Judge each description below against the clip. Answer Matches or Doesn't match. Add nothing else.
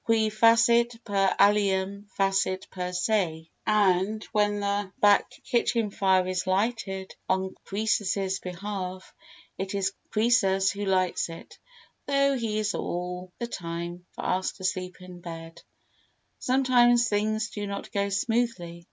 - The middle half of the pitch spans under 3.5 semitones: Matches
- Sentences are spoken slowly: Matches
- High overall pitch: Matches